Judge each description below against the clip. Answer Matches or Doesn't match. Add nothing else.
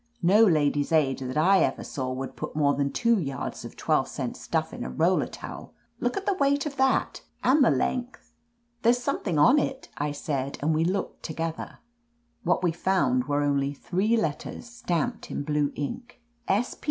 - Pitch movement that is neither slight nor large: Doesn't match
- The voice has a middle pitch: Matches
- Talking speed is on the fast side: Doesn't match